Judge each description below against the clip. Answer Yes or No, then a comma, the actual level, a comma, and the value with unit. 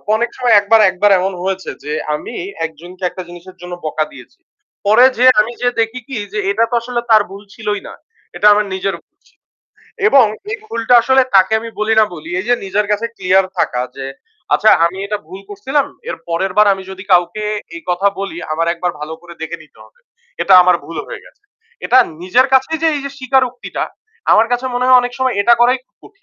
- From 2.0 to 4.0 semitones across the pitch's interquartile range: No, average, 5.1 semitones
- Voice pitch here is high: Yes, high, 210 Hz